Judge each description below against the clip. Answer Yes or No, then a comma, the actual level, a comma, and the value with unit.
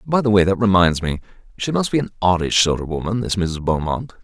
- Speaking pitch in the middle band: No, low, 100 Hz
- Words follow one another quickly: Yes, fast, 240 wpm